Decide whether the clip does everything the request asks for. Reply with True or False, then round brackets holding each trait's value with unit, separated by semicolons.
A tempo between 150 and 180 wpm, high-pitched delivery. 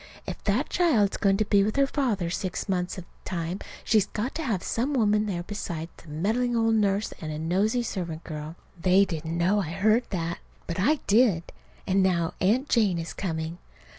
False (200 wpm; 195 Hz)